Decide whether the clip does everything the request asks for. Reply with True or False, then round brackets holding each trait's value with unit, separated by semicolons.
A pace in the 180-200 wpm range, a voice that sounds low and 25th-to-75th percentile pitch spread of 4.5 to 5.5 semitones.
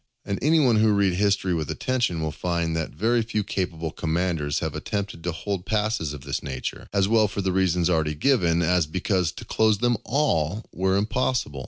True (190 wpm; 95 Hz; 4.8 semitones)